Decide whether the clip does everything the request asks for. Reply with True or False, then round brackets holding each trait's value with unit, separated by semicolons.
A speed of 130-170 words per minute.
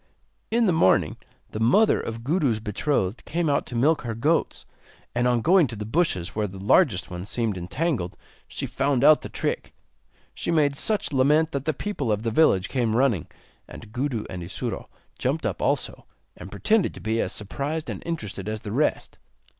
False (185 wpm)